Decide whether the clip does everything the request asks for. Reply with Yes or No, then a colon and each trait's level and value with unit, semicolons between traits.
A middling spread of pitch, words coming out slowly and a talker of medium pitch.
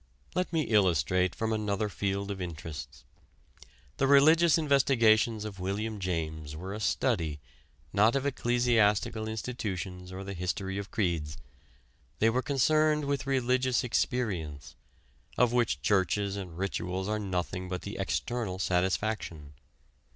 No: average, 4.9 semitones; slow, 130 wpm; low, 100 Hz